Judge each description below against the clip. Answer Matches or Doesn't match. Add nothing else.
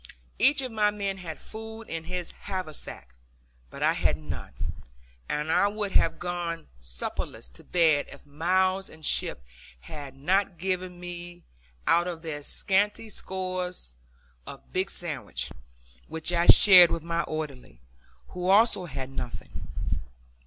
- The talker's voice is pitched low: Doesn't match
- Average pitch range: Matches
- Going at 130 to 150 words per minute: Matches